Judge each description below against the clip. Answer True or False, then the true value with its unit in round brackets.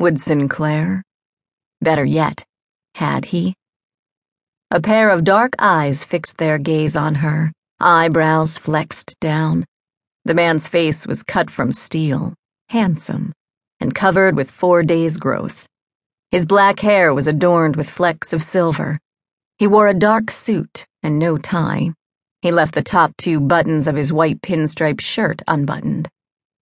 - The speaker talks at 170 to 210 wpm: False (140 wpm)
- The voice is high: False (165 Hz)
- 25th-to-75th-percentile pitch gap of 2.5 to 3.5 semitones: True (2.8 semitones)